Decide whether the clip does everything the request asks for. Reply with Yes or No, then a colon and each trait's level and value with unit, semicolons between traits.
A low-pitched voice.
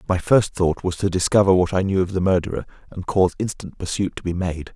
Yes: very low, 95 Hz